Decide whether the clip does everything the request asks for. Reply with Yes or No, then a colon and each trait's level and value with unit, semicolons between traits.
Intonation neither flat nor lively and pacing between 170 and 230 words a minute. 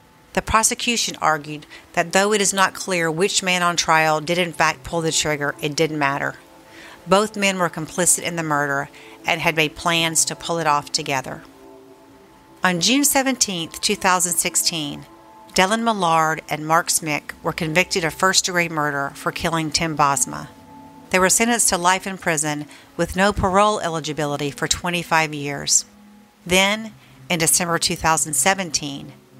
No: average, 3.8 semitones; average, 155 wpm